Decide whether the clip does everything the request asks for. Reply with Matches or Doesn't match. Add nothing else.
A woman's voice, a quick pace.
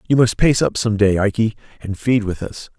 Doesn't match